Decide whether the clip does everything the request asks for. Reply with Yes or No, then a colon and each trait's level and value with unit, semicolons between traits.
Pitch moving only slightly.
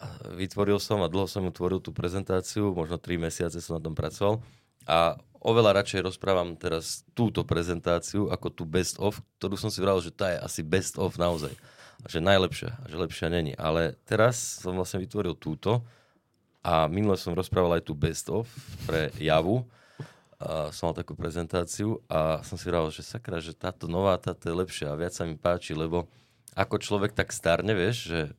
No: average, 3.5 semitones